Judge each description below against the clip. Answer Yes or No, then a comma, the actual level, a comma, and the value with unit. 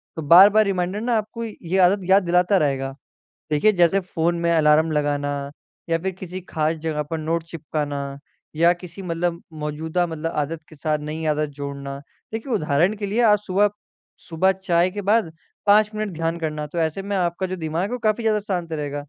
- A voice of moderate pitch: Yes, medium, 170 Hz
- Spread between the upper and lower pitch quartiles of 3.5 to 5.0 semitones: Yes, average, 4.1 semitones